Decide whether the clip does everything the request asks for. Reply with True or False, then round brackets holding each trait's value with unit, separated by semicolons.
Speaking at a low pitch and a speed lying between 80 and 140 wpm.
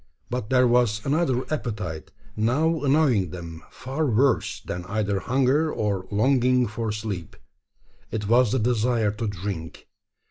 True (115 Hz; 135 wpm)